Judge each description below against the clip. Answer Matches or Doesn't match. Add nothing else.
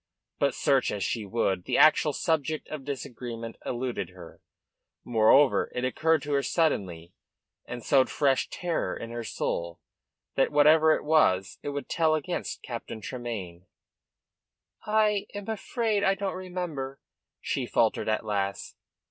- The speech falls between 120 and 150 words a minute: Matches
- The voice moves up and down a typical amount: Doesn't match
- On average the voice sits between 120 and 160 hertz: Matches